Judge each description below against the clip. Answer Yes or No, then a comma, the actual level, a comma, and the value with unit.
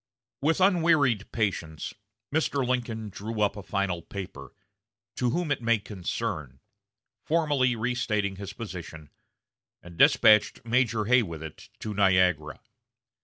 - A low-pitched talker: Yes, low, 105 Hz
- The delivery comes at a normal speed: No, slow, 120 wpm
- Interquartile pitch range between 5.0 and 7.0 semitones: Yes, wide, 5.4 semitones